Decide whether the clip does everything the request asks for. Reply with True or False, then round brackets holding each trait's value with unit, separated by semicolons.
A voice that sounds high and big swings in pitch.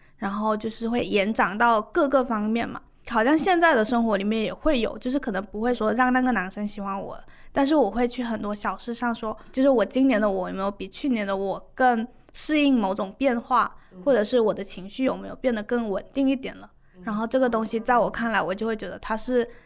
False (230 Hz; 3.6 semitones)